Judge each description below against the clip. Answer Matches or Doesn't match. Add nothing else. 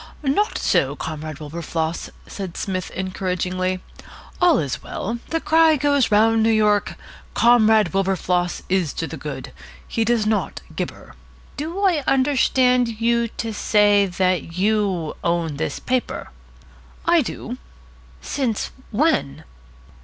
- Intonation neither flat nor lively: Doesn't match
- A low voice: Doesn't match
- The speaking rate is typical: Doesn't match